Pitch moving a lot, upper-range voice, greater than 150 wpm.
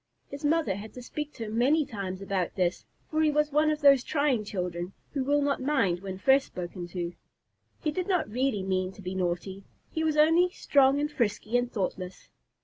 Yes: wide, 7.9 semitones; high, 245 Hz; fast, 205 wpm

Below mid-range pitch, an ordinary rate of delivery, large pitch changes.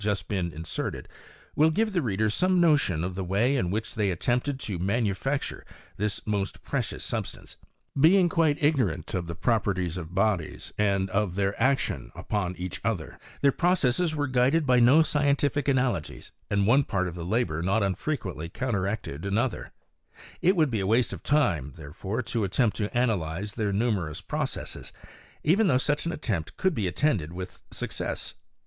Yes: low, 110 Hz; average, 165 wpm; wide, 6.9 semitones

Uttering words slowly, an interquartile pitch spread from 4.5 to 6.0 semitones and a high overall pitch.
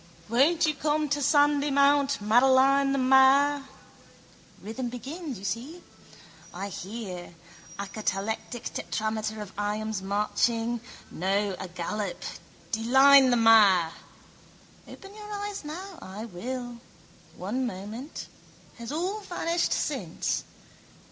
Yes: slow, 105 wpm; wide, 5.5 semitones; high, 245 Hz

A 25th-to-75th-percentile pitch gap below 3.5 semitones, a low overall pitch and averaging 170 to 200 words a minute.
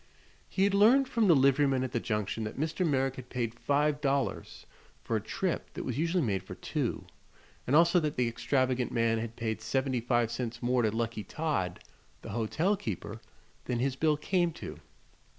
No: average, 4.9 semitones; low, 130 Hz; average, 185 wpm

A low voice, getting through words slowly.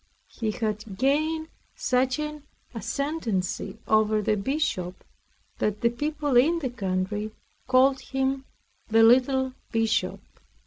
No: high, 245 Hz; slow, 115 wpm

